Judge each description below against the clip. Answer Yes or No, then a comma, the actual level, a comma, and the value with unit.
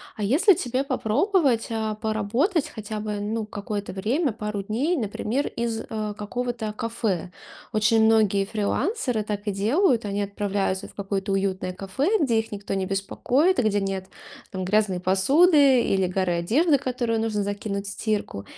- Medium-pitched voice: No, high, 215 Hz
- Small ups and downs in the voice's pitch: No, average, 3.7 semitones